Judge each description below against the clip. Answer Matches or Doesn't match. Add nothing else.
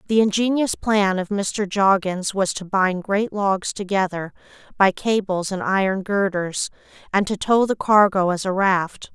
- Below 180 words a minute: Matches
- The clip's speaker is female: Matches